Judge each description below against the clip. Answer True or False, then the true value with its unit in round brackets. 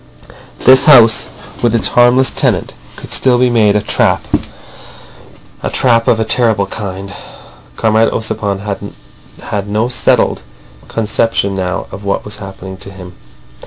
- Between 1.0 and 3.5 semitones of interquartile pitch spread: True (2.9 semitones)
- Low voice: True (110 Hz)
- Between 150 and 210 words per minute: False (135 wpm)